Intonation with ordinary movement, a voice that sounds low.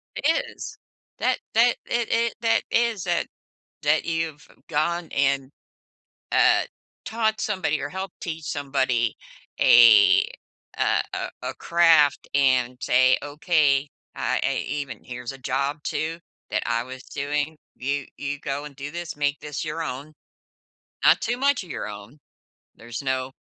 No: average, 4.2 semitones; medium, 145 Hz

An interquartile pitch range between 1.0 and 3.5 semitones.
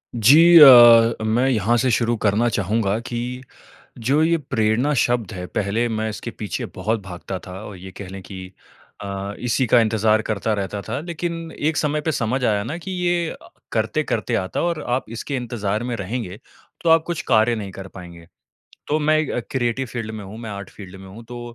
No: average, 4.6 semitones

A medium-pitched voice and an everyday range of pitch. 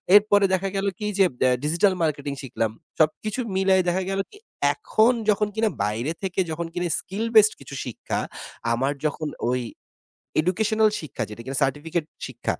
No: medium, 180 Hz; wide, 5.8 semitones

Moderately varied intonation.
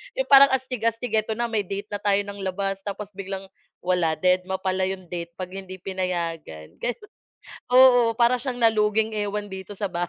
Yes: average, 3.1 semitones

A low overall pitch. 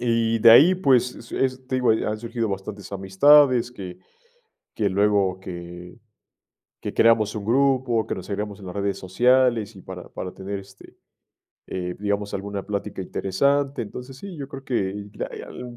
Yes: low, 105 Hz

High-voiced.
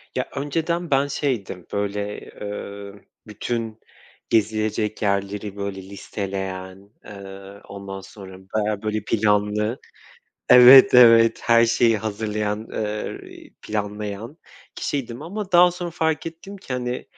No: low, 105 Hz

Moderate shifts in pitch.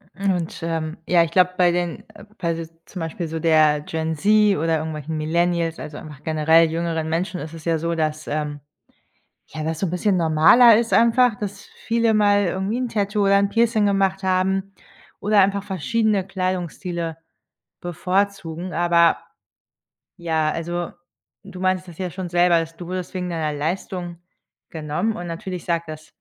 Yes: average, 3.0 semitones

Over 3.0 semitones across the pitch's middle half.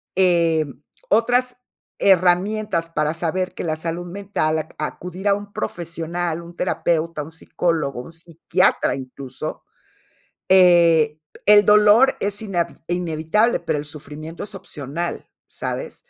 Yes: average, 3.5 semitones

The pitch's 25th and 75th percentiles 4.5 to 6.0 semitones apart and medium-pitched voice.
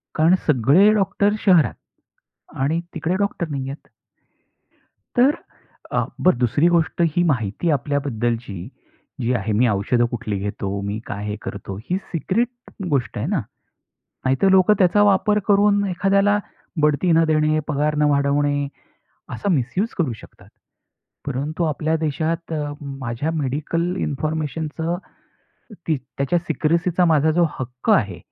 Yes: average, 5.0 semitones; medium, 155 Hz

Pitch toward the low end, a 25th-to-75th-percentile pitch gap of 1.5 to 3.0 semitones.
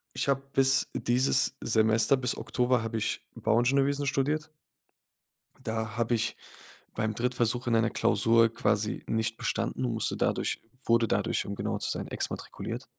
Yes: low, 115 Hz; narrow, 2.6 semitones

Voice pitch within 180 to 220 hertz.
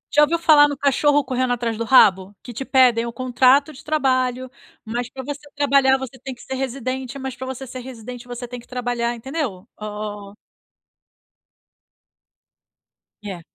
No: very high, 255 Hz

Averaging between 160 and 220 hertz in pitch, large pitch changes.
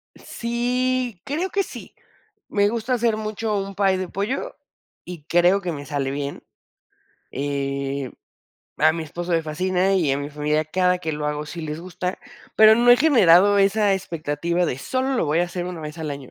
Yes: medium, 180 Hz; wide, 5.9 semitones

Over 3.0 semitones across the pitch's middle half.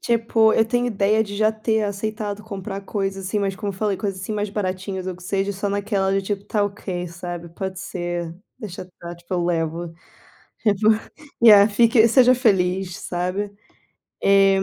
No: narrow, 2.4 semitones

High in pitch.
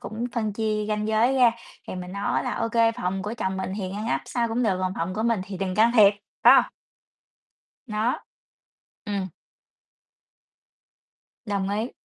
Yes: high, 210 Hz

